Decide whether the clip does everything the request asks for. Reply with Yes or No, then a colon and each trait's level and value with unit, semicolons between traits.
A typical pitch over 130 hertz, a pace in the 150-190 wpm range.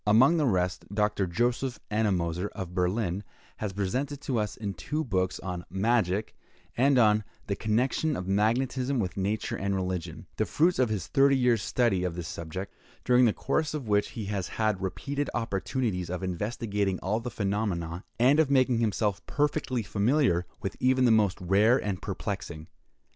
No: low, 105 Hz; average, 170 wpm